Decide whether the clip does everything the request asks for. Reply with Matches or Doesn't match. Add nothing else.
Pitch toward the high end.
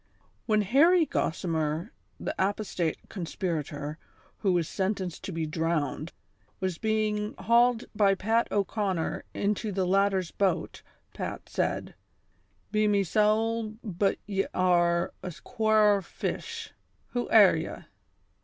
Matches